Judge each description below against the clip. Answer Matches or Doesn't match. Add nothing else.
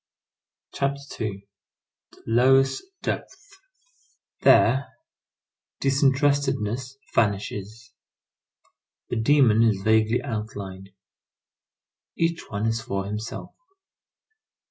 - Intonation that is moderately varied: Matches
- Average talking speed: Doesn't match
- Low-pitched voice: Matches